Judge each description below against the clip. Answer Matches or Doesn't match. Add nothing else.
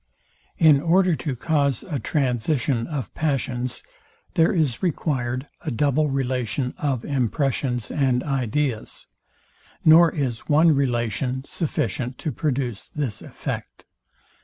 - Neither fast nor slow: Doesn't match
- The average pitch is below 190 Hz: Matches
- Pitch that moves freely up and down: Doesn't match